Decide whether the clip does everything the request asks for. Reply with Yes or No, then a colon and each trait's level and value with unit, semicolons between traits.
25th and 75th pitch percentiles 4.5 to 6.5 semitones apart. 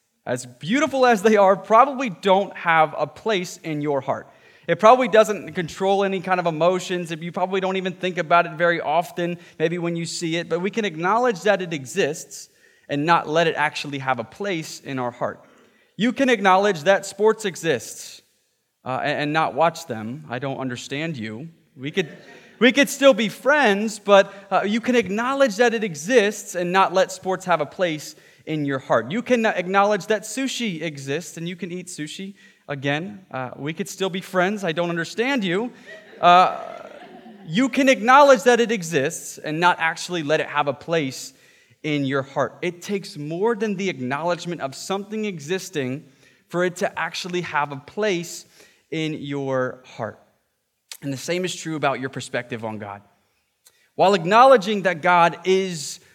Yes: average, 5.1 semitones